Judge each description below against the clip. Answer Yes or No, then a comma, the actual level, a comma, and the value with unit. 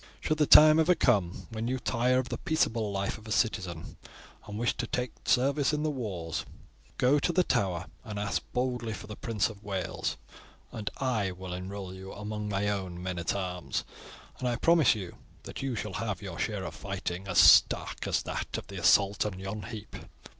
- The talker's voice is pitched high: No, low, 105 Hz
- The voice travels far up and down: No, average, 4.5 semitones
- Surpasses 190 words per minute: Yes, average, 200 wpm